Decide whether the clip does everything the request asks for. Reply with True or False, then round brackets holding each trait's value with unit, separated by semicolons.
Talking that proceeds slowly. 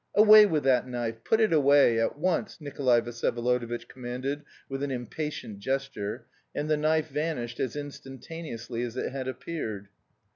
False (150 wpm)